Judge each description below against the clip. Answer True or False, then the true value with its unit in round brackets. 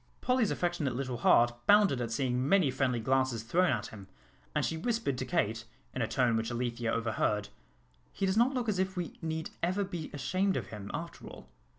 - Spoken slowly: False (200 wpm)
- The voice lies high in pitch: False (135 Hz)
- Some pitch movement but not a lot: False (7.9 semitones)